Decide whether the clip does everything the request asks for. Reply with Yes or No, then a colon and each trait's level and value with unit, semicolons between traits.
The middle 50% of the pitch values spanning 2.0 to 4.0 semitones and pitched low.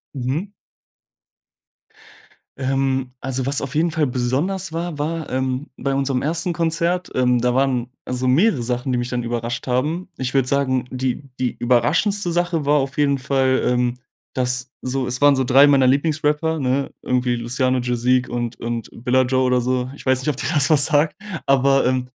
Yes: average, 2.7 semitones; low, 130 Hz